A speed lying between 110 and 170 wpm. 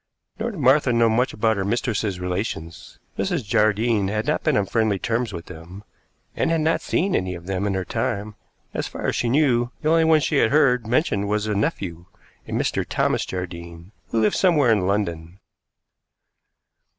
No: average, 185 wpm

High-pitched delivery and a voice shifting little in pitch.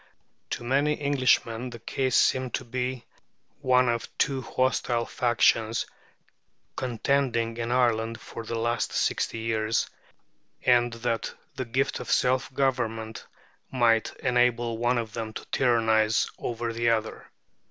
No: low, 120 Hz; narrow, 1.9 semitones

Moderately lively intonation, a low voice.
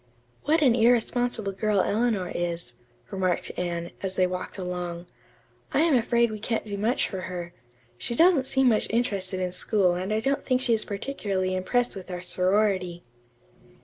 No: average, 4.6 semitones; high, 200 Hz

